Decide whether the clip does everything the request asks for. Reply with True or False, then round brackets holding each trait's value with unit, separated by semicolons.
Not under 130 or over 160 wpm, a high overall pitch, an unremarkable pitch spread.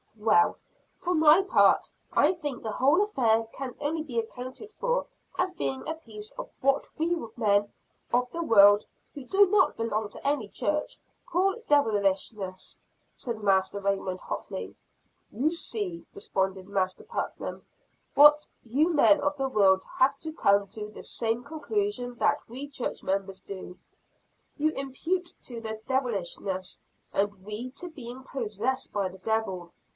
False (150 wpm; 245 Hz; 6.7 semitones)